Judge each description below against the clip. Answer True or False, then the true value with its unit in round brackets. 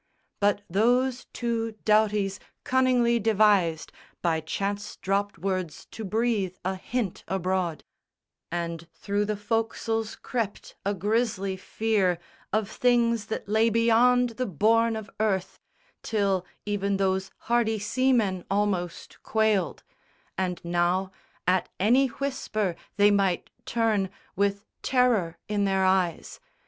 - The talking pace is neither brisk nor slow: False (115 wpm)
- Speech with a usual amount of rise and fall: True (3.1 semitones)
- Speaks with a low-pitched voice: False (205 Hz)